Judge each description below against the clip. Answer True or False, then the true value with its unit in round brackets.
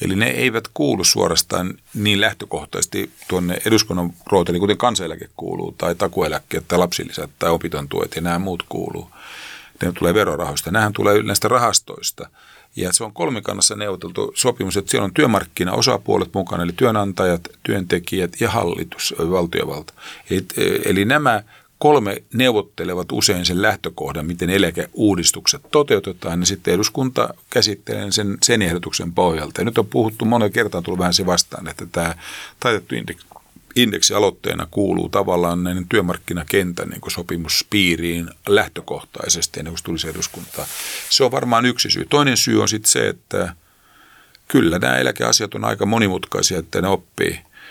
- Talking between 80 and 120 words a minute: False (140 wpm)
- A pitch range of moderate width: True (3.7 semitones)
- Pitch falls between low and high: False (95 Hz)